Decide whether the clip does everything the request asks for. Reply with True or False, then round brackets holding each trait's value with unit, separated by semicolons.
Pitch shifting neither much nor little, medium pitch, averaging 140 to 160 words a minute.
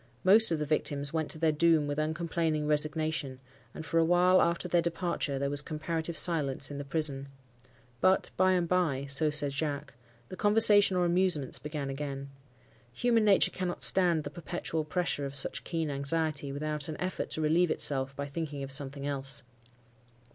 False (3.4 semitones; 155 Hz; 170 wpm)